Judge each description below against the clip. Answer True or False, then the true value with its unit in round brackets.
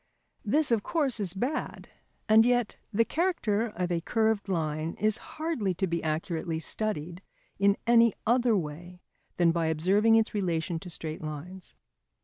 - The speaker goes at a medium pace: True (150 wpm)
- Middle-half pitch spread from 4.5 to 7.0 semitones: True (5.3 semitones)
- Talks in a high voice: True (200 Hz)